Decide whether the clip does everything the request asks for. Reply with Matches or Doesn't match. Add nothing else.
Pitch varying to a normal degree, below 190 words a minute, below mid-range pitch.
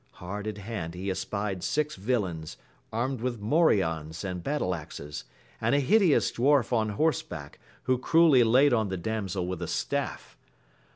Doesn't match